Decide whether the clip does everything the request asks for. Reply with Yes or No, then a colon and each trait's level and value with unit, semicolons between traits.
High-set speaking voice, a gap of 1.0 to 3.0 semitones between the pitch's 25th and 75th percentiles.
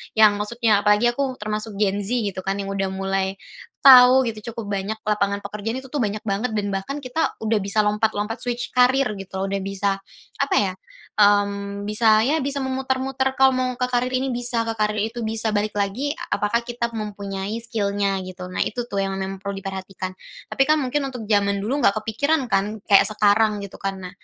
No: high, 215 Hz; average, 3.6 semitones